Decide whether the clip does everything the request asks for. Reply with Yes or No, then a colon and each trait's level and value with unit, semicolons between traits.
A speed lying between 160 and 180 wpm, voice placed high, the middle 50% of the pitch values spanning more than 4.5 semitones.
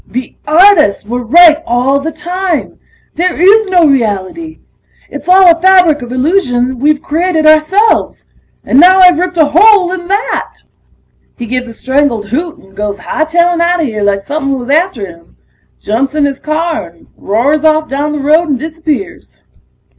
Yes: average, 165 wpm; very high, 310 Hz; wide, 5.5 semitones